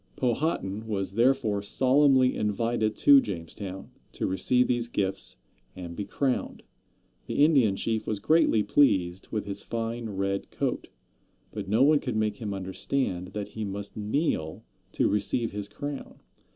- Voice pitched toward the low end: Yes, low, 110 Hz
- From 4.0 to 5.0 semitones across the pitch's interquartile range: Yes, average, 4.5 semitones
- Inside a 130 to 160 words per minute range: Yes, average, 145 wpm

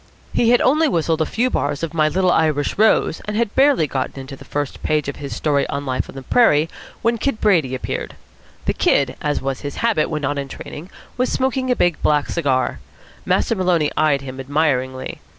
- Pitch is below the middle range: No, medium, 155 Hz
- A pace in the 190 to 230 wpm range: Yes, fast, 205 wpm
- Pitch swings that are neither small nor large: No, wide, 7.0 semitones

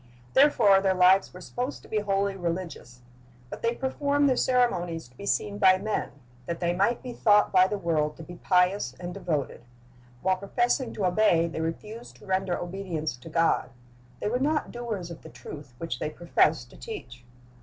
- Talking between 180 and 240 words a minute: Yes, average, 185 wpm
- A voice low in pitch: No, medium, 185 Hz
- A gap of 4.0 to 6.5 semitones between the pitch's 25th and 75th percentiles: Yes, average, 4.3 semitones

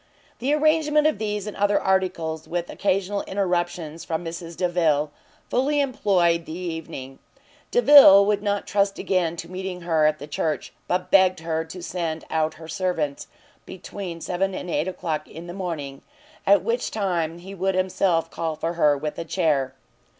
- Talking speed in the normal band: Yes, average, 165 wpm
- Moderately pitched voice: Yes, medium, 175 Hz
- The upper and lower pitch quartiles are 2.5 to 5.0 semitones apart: Yes, average, 3.3 semitones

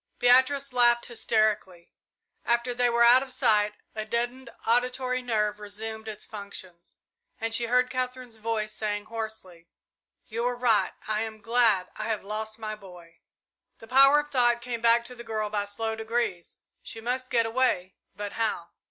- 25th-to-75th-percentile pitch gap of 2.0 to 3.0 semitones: Yes, narrow, 2.6 semitones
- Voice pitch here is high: Yes, high, 225 Hz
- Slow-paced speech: No, average, 165 wpm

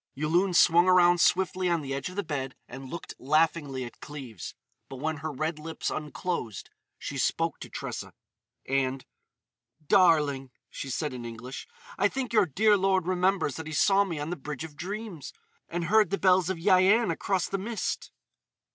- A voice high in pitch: No, medium, 165 Hz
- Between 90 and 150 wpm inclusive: No, average, 175 wpm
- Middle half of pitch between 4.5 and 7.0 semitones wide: Yes, average, 4.8 semitones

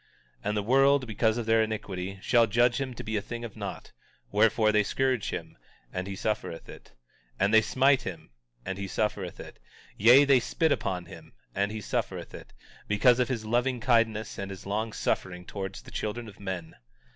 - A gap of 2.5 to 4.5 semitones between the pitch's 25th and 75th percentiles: Yes, average, 3.4 semitones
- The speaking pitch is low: Yes, low, 110 Hz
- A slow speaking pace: No, average, 195 wpm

